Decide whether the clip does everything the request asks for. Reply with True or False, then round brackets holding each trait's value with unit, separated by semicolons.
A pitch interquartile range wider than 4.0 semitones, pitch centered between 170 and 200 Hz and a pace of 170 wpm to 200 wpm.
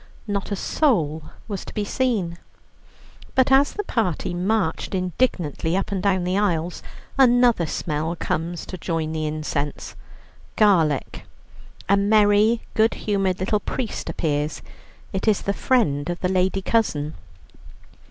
False (4.9 semitones; 190 Hz; 135 wpm)